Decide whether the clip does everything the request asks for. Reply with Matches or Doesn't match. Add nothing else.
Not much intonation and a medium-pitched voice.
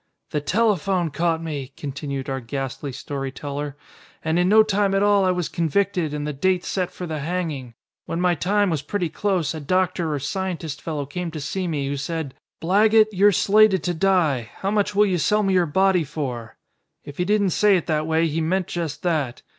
Doesn't match